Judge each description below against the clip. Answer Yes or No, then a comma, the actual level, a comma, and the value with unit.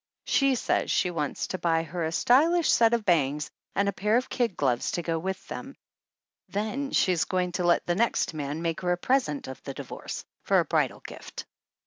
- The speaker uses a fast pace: Yes, fast, 215 wpm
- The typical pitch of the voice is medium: Yes, medium, 180 Hz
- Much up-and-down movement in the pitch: Yes, wide, 5.8 semitones